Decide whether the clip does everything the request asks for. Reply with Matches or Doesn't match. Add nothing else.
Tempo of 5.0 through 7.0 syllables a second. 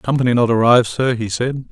Matches